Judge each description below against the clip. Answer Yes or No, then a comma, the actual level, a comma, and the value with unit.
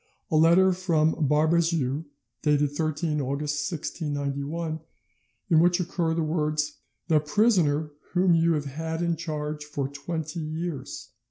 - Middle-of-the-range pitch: Yes, medium, 155 Hz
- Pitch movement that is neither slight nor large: No, narrow, 2.2 semitones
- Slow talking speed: Yes, slow, 125 wpm